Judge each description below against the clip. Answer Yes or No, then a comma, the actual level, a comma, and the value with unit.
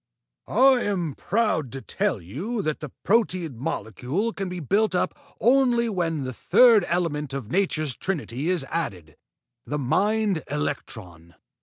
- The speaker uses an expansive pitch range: Yes, wide, 7.2 semitones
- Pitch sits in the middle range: Yes, medium, 170 Hz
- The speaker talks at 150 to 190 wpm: No, average, 140 wpm